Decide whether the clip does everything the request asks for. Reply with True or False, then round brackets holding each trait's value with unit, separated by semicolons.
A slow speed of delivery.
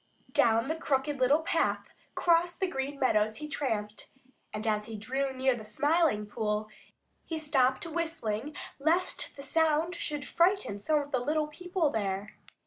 False (155 wpm)